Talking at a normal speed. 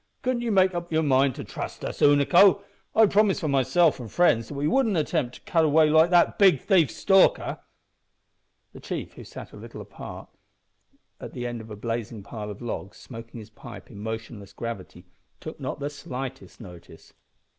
Yes: average, 190 wpm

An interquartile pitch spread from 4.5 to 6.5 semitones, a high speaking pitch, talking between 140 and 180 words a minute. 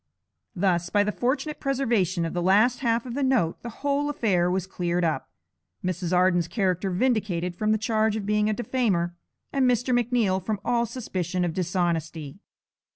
Yes: average, 5.3 semitones; high, 200 Hz; average, 170 wpm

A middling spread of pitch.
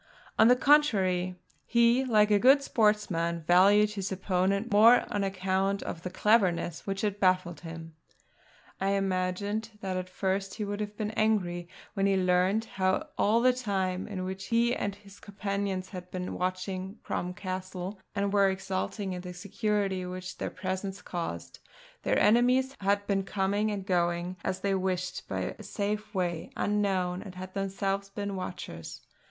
No: narrow, 2.1 semitones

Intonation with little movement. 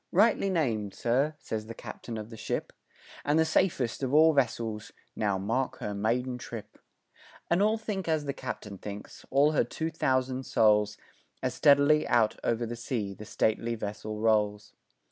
No: wide, 5.4 semitones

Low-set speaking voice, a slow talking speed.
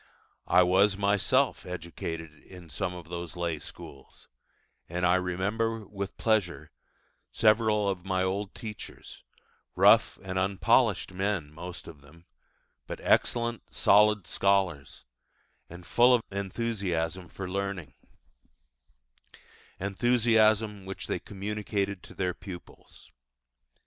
Yes: very low, 95 Hz; slow, 110 wpm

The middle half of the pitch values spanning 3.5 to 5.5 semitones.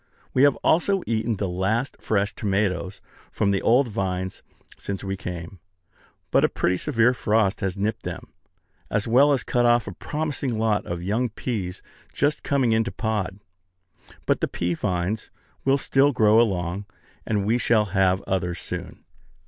Yes: average, 3.9 semitones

